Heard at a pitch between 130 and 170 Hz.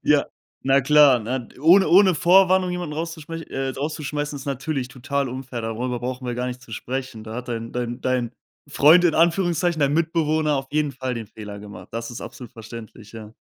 Yes: low, 135 Hz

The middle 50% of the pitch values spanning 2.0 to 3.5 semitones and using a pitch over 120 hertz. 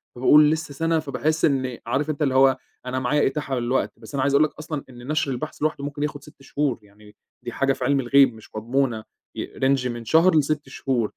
Yes: average, 2.9 semitones; low, 135 Hz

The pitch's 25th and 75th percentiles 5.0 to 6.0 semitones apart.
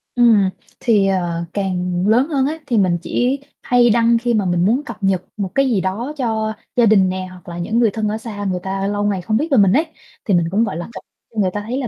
No: average, 4.0 semitones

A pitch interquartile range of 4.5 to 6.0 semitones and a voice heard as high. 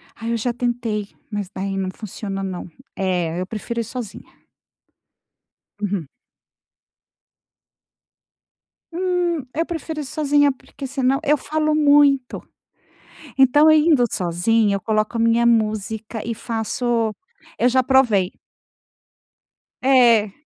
Yes: average, 4.9 semitones; high, 235 Hz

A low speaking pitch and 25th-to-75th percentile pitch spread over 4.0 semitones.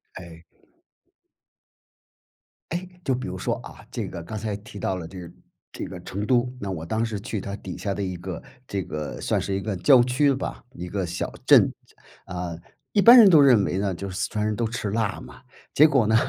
Yes: low, 100 Hz; average, 4.7 semitones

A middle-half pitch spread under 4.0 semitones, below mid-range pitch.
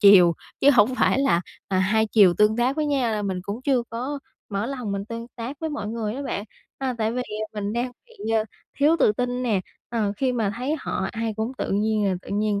No: average, 3.6 semitones; high, 225 Hz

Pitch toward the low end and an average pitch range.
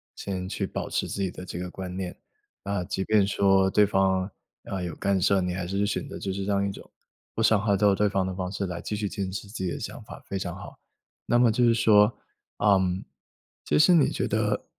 No: very low, 95 Hz; narrow, 1.7 semitones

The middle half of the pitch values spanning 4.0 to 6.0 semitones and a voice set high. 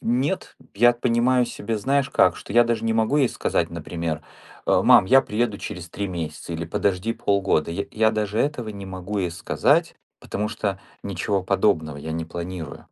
No: average, 4.7 semitones; low, 100 Hz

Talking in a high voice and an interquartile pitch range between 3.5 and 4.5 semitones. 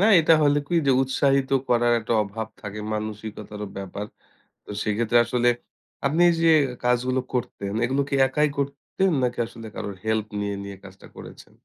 No: low, 120 Hz; average, 4.1 semitones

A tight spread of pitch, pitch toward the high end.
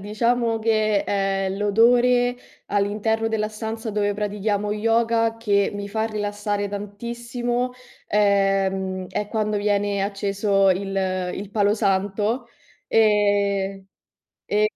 Yes: narrow, 1.9 semitones; high, 210 Hz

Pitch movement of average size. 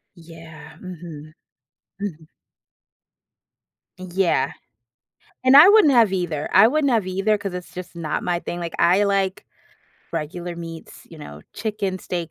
Yes: average, 3.4 semitones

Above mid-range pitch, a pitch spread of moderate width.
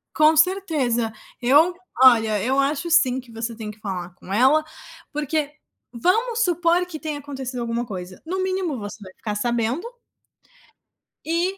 No: very high, 270 Hz; wide, 6.5 semitones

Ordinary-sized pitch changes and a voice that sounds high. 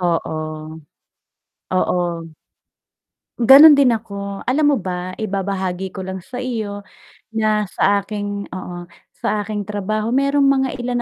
Yes: average, 4.4 semitones; high, 205 Hz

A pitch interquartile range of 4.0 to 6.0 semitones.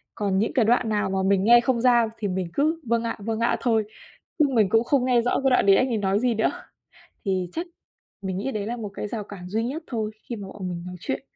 No: average, 3.5 semitones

